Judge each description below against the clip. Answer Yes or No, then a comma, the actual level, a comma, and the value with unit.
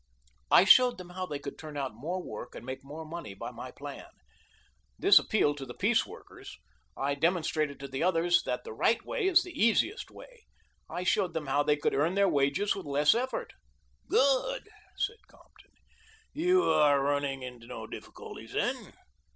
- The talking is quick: No, average, 180 wpm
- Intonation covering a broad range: Yes, wide, 6.6 semitones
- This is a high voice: No, medium, 155 Hz